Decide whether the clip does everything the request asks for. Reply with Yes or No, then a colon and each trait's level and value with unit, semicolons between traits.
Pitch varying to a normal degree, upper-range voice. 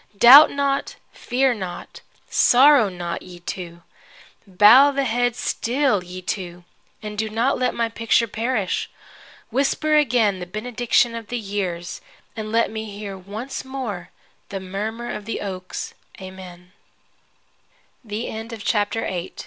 Yes: average, 4.3 semitones; high, 220 Hz